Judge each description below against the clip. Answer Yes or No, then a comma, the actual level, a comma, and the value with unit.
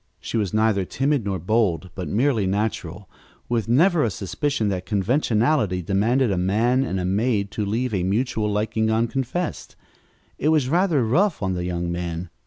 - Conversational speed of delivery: Yes, average, 170 wpm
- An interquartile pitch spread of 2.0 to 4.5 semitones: No, average, 5.1 semitones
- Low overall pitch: Yes, low, 110 Hz